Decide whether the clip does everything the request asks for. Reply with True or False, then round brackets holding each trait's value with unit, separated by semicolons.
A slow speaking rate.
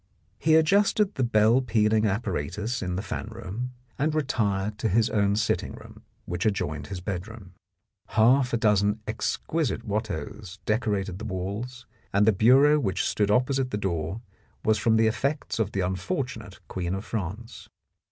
False (155 wpm)